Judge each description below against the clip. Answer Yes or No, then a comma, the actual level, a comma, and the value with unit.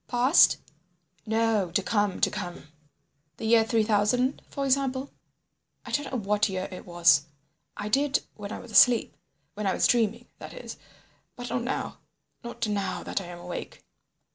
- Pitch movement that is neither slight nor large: Yes, average, 3.7 semitones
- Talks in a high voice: Yes, high, 220 Hz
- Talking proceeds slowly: No, average, 160 wpm